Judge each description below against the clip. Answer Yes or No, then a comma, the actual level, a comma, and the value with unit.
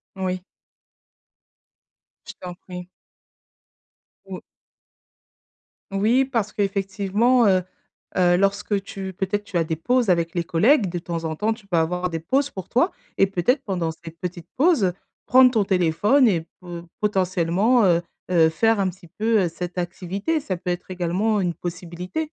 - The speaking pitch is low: No, medium, 185 Hz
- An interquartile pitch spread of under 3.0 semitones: No, average, 3.5 semitones